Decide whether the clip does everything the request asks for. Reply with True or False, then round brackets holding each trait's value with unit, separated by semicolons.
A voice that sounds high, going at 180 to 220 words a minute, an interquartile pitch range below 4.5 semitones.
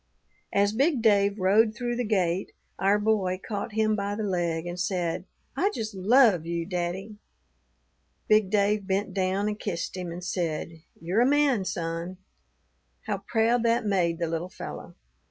False (200 Hz; 160 wpm; 3.6 semitones)